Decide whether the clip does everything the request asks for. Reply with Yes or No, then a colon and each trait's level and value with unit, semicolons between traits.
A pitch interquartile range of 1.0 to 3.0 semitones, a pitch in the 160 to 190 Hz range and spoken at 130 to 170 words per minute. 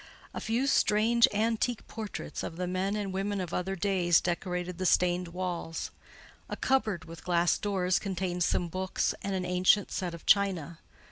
Yes: narrow, 2.4 semitones; medium, 185 Hz; average, 165 wpm